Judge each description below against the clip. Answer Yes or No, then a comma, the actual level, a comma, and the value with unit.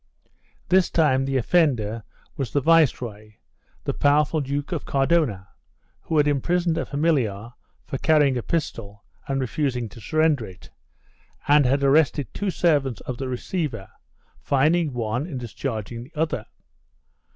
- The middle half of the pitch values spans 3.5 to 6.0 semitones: Yes, average, 4.6 semitones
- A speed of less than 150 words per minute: Yes, average, 140 wpm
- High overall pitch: No, medium, 140 Hz